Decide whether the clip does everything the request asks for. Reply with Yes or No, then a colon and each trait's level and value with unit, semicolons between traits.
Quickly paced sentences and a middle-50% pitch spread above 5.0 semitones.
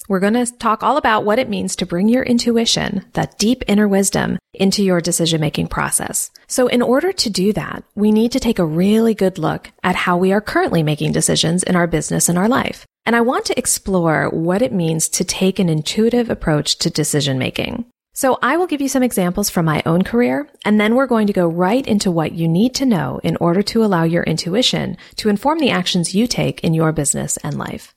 Yes: fast, 225 wpm; wide, 5.4 semitones